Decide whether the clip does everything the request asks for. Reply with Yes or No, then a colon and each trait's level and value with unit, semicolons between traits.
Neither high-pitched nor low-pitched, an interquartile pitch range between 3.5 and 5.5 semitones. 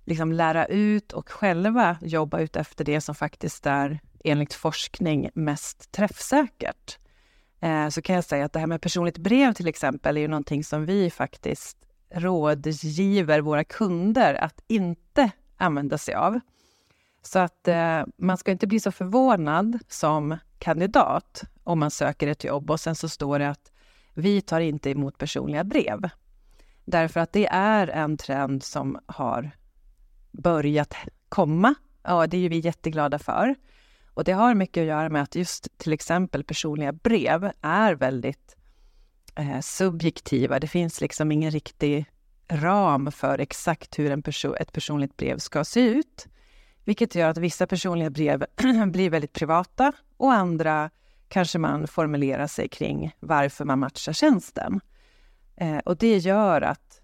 Yes: medium, 165 Hz; average, 4.4 semitones